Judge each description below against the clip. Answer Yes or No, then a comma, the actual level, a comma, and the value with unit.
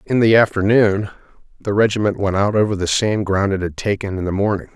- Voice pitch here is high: No, low, 100 Hz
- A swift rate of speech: Yes, fast, 215 wpm